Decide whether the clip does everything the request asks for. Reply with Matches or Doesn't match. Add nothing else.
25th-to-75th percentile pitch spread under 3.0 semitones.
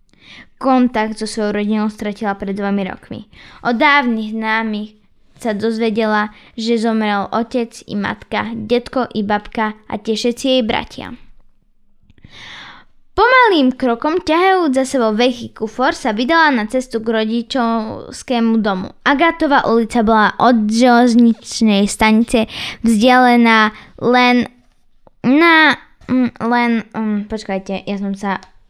Matches